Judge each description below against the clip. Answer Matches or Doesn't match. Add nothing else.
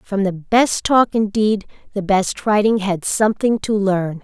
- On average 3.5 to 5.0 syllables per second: Matches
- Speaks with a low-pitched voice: Doesn't match